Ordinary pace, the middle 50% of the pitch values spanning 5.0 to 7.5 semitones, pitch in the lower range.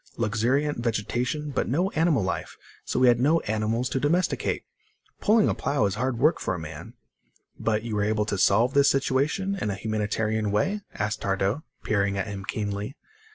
Yes: average, 180 wpm; average, 5.3 semitones; low, 115 Hz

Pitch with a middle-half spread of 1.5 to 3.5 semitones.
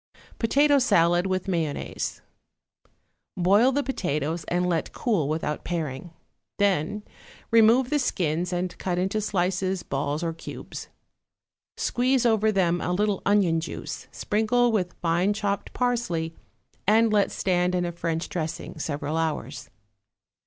No: average, 4.4 semitones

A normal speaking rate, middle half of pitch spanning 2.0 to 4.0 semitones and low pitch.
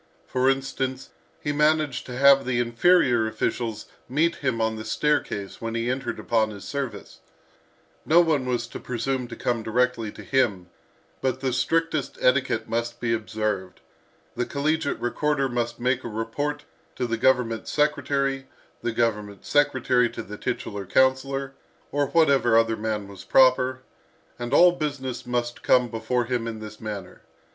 Yes: average, 155 wpm; average, 3.3 semitones; low, 125 Hz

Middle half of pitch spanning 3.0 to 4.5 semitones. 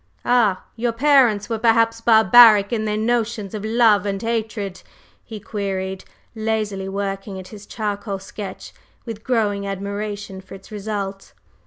No: narrow, 2.4 semitones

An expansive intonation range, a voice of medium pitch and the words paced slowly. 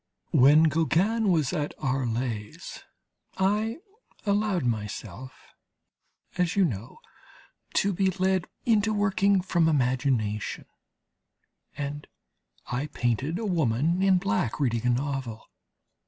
Yes: wide, 7.5 semitones; medium, 150 Hz; slow, 105 wpm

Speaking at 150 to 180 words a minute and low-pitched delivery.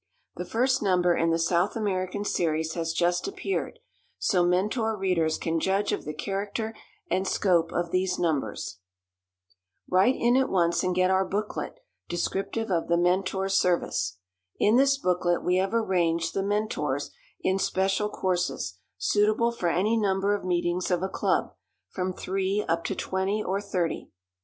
No: average, 155 wpm; medium, 185 Hz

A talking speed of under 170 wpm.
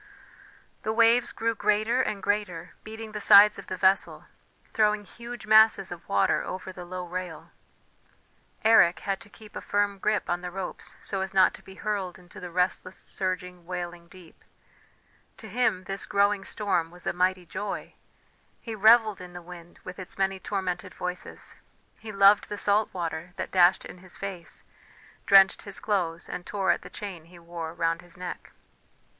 No: average, 175 wpm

